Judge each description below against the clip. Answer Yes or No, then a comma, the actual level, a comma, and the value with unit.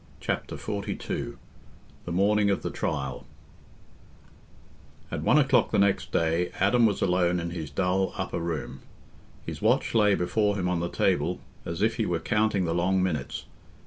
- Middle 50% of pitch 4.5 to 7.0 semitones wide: No, average, 3.3 semitones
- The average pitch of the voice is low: Yes, very low, 95 Hz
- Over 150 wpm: Yes, average, 160 wpm